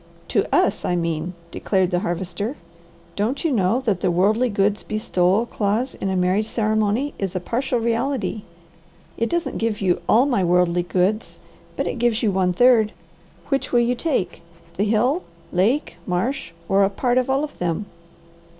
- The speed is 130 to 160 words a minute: No, average, 170 wpm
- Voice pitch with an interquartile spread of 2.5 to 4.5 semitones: No, average, 4.9 semitones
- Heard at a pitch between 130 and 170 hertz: No, high, 215 Hz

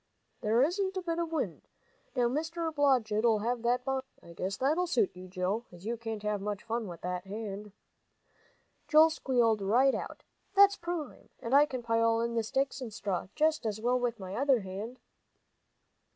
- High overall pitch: Yes, high, 235 Hz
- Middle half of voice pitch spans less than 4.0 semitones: No, average, 5.3 semitones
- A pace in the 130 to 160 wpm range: No, average, 180 wpm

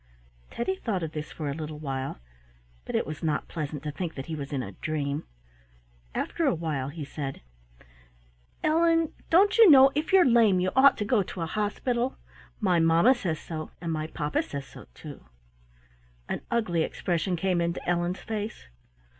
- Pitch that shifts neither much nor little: No, wide, 7.4 semitones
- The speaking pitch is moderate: Yes, medium, 170 Hz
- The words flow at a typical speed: Yes, average, 180 wpm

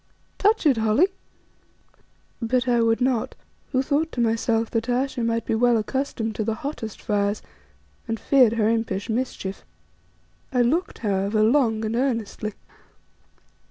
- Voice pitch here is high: Yes, high, 230 Hz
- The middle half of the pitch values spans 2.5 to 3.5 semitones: Yes, average, 2.8 semitones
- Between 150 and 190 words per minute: No, average, 140 wpm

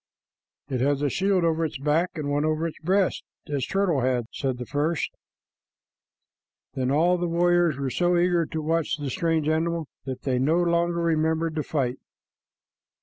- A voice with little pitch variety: No, average, 3.1 semitones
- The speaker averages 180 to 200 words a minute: No, average, 170 wpm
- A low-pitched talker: No, medium, 160 Hz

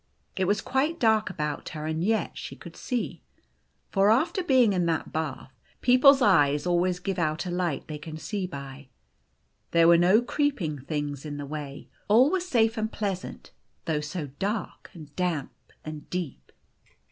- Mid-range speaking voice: Yes, medium, 180 Hz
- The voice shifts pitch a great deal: Yes, wide, 6.3 semitones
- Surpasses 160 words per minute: Yes, average, 180 wpm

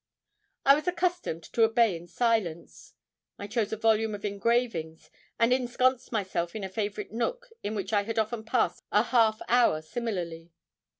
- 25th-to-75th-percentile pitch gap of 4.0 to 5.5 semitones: No, average, 3.4 semitones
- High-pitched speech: Yes, high, 220 Hz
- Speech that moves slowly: No, average, 165 wpm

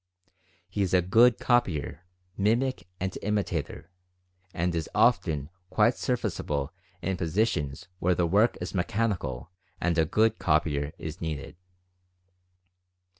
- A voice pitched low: Yes, very low, 90 Hz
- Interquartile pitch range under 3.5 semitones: No, average, 5.0 semitones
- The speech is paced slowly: Yes, slow, 125 wpm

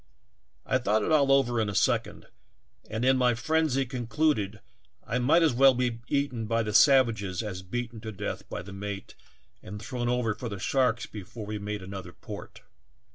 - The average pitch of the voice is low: Yes, low, 115 Hz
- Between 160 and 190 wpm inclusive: Yes, average, 185 wpm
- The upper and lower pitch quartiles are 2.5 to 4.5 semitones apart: Yes, average, 3.8 semitones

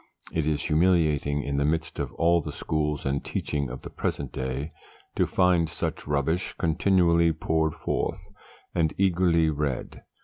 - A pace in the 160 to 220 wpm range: No, average, 150 wpm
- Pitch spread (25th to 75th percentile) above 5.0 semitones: No, average, 2.7 semitones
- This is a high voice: No, very low, 80 Hz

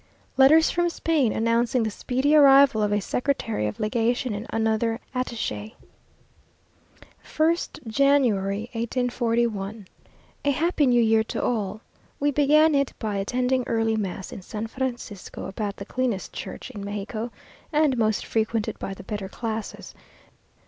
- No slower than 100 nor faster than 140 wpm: Yes, slow, 135 wpm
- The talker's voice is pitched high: Yes, high, 230 Hz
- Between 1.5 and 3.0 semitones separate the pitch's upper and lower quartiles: No, average, 3.9 semitones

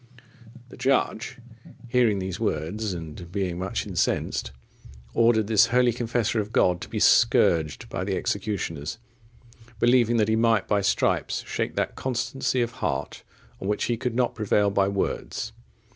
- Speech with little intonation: No, average, 3.9 semitones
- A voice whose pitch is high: No, low, 105 Hz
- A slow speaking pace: No, average, 150 wpm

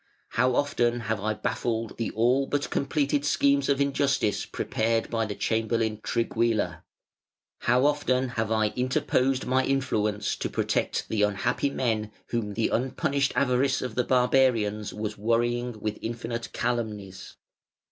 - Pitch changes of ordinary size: Yes, average, 3.3 semitones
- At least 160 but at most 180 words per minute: No, slow, 135 wpm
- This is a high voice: No, low, 120 Hz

